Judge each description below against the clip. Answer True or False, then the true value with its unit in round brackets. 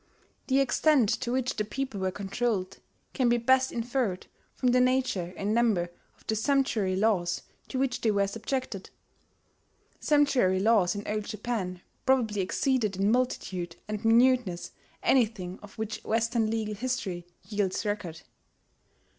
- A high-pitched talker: True (220 Hz)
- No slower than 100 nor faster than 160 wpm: True (140 wpm)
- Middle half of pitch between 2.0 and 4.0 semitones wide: False (4.4 semitones)